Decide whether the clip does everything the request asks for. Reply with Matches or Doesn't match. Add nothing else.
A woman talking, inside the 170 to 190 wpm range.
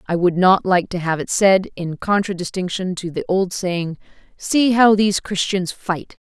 Matches